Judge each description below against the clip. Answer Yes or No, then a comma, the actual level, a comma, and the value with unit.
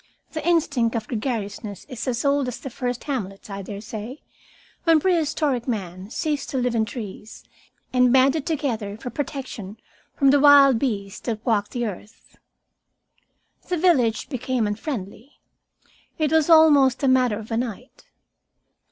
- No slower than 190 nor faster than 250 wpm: No, average, 145 wpm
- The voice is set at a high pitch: Yes, very high, 250 Hz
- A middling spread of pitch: Yes, average, 4.7 semitones